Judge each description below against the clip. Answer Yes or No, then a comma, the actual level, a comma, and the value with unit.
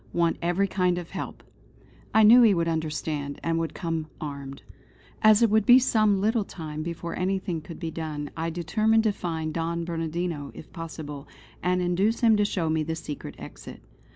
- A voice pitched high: No, medium, 170 Hz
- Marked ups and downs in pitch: No, average, 3.8 semitones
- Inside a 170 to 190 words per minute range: Yes, average, 180 wpm